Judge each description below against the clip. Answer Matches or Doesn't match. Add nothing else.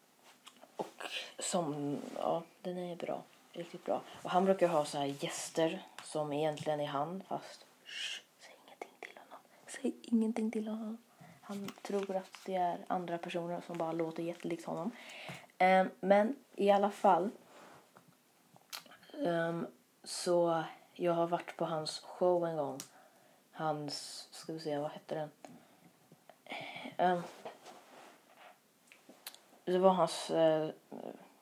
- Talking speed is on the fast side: Doesn't match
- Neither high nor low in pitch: Matches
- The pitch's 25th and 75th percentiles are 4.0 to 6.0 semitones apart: Doesn't match